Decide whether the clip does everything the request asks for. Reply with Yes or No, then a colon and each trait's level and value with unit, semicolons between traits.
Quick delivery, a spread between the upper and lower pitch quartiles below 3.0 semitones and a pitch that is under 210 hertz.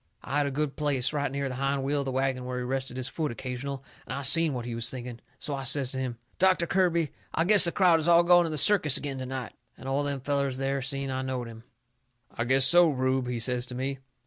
Yes: fast, 265 wpm; narrow, 2.4 semitones; low, 135 Hz